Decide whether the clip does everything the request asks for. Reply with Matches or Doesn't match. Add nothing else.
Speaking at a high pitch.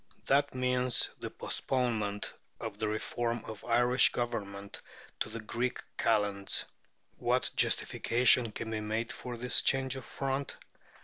Doesn't match